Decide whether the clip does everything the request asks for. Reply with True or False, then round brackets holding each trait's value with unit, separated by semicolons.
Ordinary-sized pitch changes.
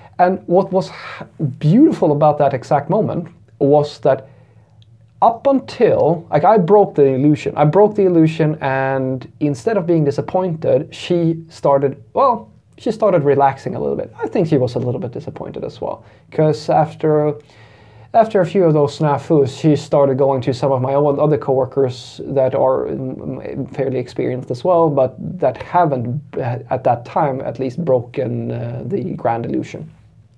True (4.1 semitones)